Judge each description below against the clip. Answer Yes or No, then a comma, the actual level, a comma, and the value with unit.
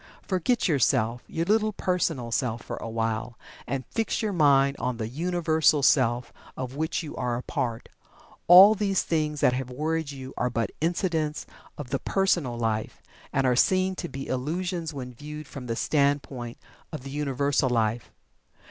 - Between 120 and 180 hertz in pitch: Yes, medium, 140 Hz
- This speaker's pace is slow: No, average, 165 wpm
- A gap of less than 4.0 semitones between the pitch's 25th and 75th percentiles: No, average, 4.9 semitones